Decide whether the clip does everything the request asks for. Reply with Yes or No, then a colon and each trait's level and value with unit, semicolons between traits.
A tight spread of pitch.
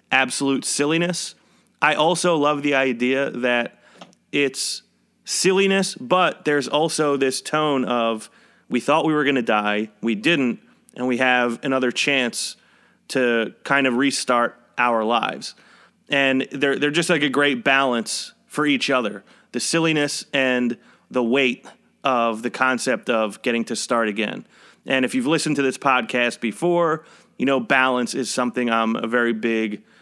No: average, 3.4 semitones